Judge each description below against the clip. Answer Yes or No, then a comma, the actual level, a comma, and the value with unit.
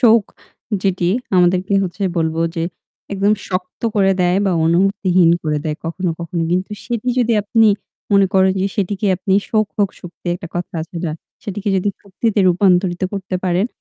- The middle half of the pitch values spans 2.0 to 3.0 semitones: Yes, narrow, 2.4 semitones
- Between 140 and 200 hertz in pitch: Yes, medium, 185 Hz